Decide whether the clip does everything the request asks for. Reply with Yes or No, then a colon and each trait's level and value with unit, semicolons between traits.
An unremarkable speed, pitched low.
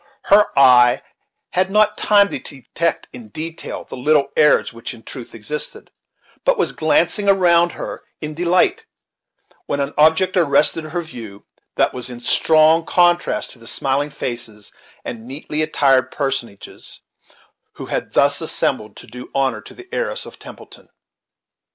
No: average, 150 wpm; medium, 150 Hz